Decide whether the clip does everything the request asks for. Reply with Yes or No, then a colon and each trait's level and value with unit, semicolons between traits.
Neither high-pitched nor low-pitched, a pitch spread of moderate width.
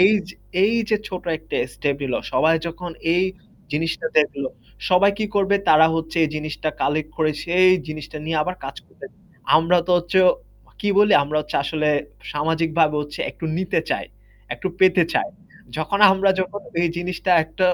Yes: medium, 165 Hz; average, 3.2 semitones